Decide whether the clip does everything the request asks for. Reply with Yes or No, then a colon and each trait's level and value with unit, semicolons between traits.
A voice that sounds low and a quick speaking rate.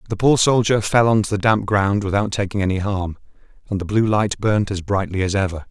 Yes: low, 100 Hz; fast, 230 wpm